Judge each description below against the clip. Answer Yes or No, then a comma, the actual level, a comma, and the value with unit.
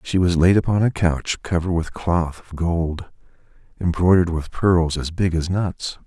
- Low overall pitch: Yes, very low, 85 Hz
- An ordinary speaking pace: Yes, average, 180 wpm